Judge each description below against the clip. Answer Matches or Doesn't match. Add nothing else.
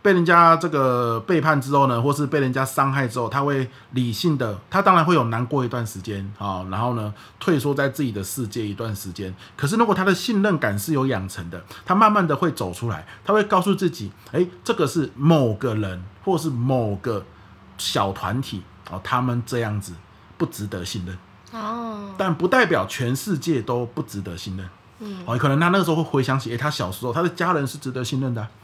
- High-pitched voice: Doesn't match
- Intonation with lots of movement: Matches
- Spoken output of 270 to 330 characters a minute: Matches